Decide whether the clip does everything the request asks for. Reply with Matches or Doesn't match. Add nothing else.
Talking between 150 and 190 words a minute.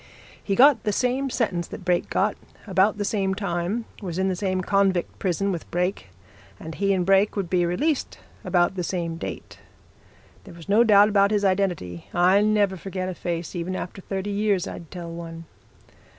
Matches